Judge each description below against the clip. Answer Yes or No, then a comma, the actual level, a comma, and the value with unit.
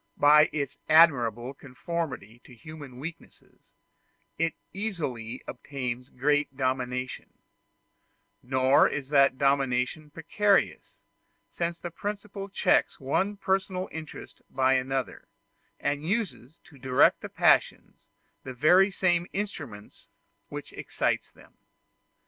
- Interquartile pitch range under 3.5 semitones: No, average, 4.8 semitones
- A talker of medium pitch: Yes, medium, 145 Hz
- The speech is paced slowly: Yes, slow, 105 wpm